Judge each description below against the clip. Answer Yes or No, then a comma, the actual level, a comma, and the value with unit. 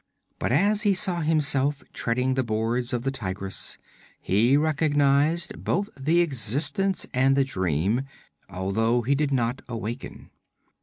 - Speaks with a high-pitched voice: No, low, 135 Hz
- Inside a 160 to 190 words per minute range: No, slow, 135 wpm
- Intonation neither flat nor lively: Yes, average, 4.7 semitones